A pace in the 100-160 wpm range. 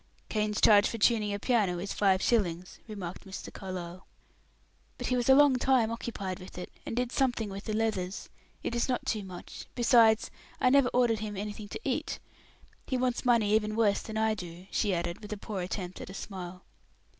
No: average, 200 wpm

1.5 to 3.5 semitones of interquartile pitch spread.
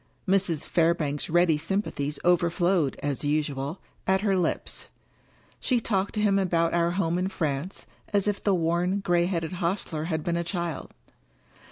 Yes: average, 2.9 semitones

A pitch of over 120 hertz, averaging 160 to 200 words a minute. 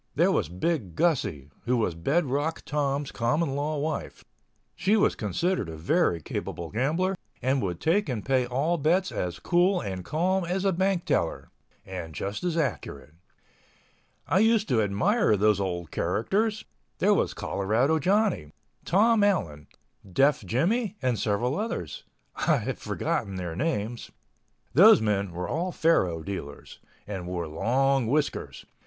No: low, 135 Hz; average, 145 wpm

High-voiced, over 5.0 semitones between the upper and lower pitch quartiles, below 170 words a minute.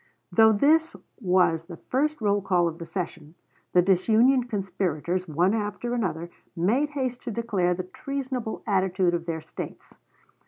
Yes: high, 195 Hz; wide, 5.5 semitones; average, 155 wpm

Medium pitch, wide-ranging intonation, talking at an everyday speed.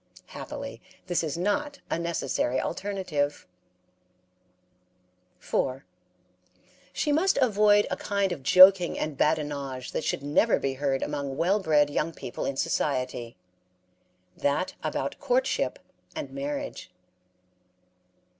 No: medium, 165 Hz; wide, 6.5 semitones; slow, 110 wpm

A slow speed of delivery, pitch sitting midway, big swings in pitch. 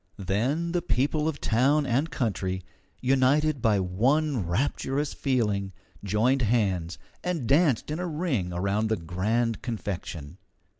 No: slow, 130 wpm; low, 120 Hz; wide, 6.6 semitones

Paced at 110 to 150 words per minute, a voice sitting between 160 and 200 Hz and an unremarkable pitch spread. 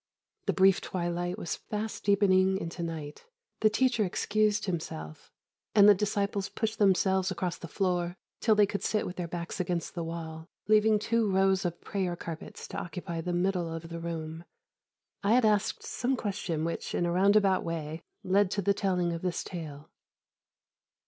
No: average, 170 wpm; medium, 185 Hz; average, 3.2 semitones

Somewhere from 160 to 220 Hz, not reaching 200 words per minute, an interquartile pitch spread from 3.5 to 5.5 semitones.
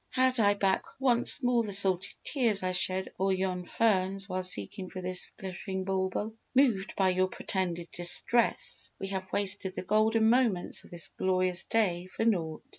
No: high, 190 Hz; average, 170 wpm; average, 2.9 semitones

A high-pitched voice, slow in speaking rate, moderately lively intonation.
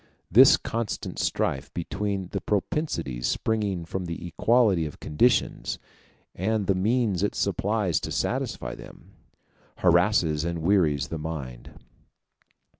No: very low, 95 Hz; slow, 115 wpm; average, 4.6 semitones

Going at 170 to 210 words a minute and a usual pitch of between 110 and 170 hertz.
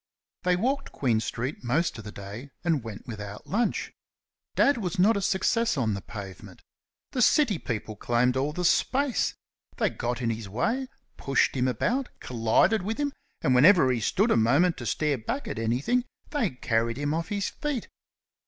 Yes: average, 180 wpm; medium, 140 Hz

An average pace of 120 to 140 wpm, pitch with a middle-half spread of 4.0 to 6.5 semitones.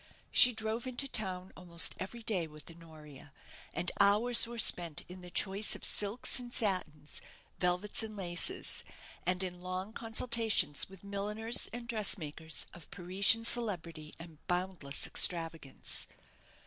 Yes: slow, 135 wpm; average, 4.6 semitones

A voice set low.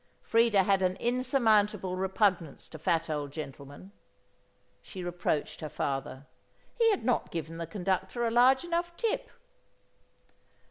No: high, 190 Hz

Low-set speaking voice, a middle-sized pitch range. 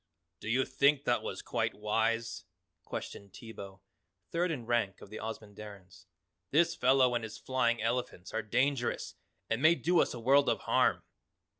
Yes: low, 115 Hz; average, 3.7 semitones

